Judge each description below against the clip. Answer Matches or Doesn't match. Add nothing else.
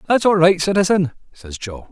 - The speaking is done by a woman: Doesn't match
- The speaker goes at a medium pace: Matches